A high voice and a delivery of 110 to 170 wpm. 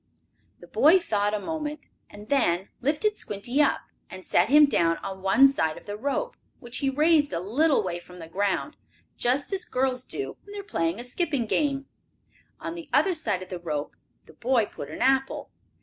No: very high, 255 Hz; average, 195 wpm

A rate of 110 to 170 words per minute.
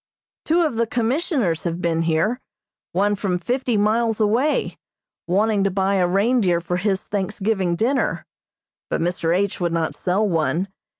Yes: average, 155 wpm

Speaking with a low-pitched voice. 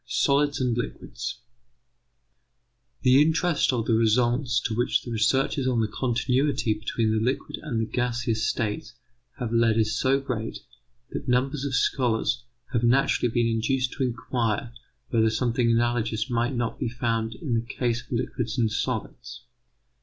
Yes: low, 120 Hz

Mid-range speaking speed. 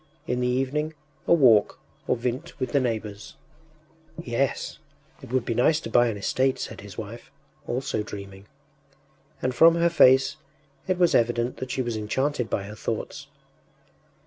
Yes: average, 160 wpm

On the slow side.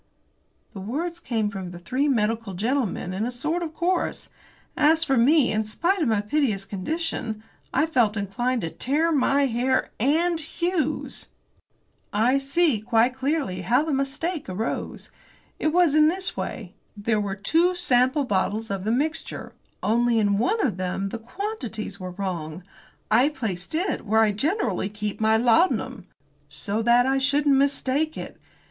No: average, 160 wpm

